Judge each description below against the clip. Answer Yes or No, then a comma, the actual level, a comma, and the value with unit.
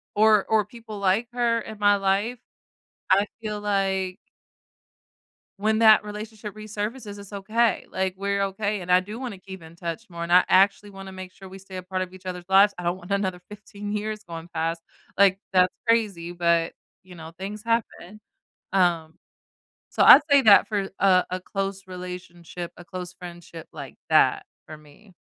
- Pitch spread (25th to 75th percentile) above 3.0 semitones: No, average, 2.7 semitones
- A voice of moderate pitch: No, high, 195 Hz